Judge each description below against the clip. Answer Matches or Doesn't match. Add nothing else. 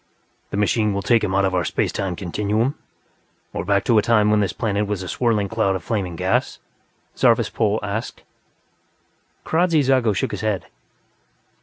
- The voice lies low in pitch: Matches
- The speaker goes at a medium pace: Matches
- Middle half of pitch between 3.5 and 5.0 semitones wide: Doesn't match